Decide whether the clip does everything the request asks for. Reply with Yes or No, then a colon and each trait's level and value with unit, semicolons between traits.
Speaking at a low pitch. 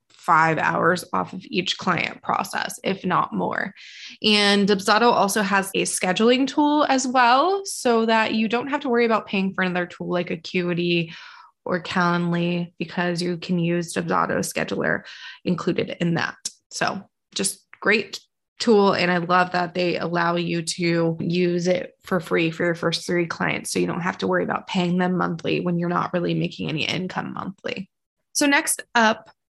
No: medium, 180 Hz